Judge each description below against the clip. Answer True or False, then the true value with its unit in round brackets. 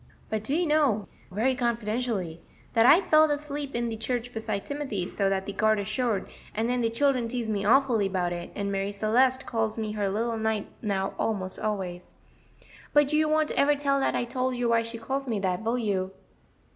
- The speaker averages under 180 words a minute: False (200 wpm)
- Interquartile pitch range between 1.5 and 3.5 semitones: False (4.2 semitones)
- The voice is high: True (225 Hz)